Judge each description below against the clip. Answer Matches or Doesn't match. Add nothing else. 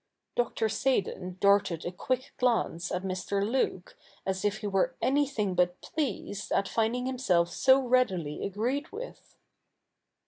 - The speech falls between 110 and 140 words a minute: Matches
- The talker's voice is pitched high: Matches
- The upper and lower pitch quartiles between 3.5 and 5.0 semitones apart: Doesn't match